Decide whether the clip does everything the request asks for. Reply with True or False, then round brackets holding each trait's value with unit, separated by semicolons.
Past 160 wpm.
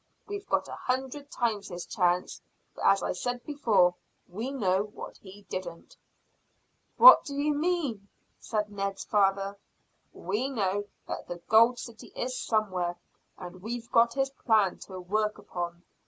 False (150 wpm)